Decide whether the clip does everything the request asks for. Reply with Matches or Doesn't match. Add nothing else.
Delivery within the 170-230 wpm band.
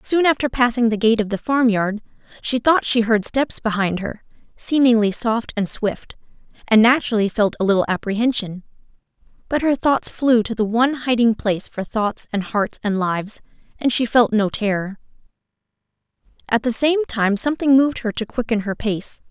Matches